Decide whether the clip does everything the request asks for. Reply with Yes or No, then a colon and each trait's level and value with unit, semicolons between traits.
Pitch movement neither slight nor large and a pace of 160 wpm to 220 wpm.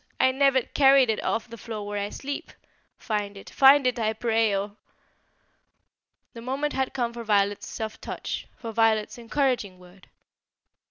Yes: average, 3.9 semitones; average, 165 wpm